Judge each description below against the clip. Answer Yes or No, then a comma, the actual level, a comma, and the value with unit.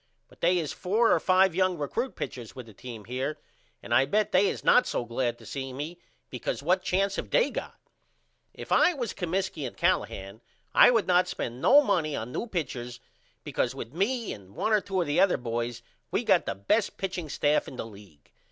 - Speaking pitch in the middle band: Yes, medium, 155 Hz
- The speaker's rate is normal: No, fast, 210 wpm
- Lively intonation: Yes, wide, 8.0 semitones